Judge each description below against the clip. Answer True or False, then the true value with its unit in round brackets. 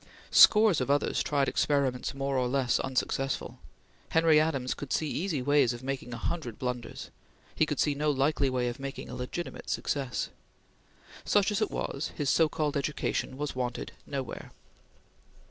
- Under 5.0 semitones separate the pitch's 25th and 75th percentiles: True (2.8 semitones)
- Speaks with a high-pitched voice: False (140 Hz)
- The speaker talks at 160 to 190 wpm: True (165 wpm)